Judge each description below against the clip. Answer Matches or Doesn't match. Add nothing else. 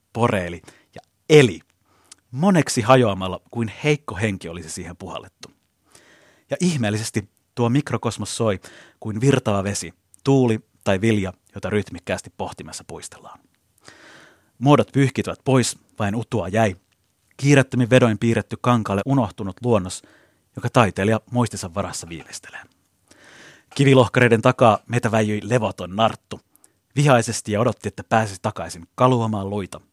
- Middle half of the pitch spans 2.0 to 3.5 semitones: Doesn't match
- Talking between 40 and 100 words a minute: Doesn't match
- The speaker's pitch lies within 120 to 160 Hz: Doesn't match